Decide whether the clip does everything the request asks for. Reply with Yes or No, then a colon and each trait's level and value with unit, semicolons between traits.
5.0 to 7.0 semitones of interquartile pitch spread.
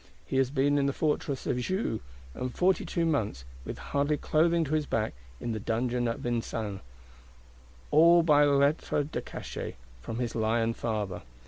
Yes: average, 5.3 semitones